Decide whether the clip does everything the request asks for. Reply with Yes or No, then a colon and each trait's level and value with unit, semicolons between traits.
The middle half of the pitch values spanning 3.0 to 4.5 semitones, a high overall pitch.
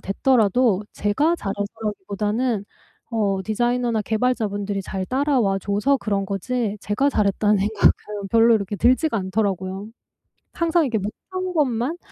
Yes: average, 3.8 semitones; high, 215 Hz